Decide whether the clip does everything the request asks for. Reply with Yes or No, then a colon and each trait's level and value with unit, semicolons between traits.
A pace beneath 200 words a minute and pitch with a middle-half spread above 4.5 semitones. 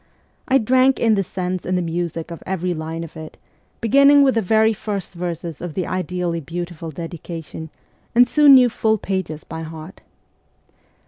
Yes: average, 170 wpm; average, 4.9 semitones